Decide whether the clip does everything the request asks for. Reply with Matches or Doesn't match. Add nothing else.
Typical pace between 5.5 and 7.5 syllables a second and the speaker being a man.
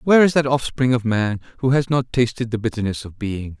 Matches